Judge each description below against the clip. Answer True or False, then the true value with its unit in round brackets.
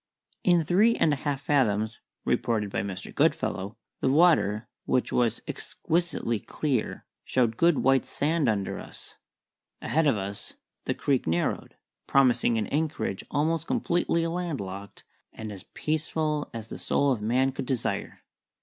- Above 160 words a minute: False (140 wpm)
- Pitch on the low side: True (130 Hz)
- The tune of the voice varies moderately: False (6.2 semitones)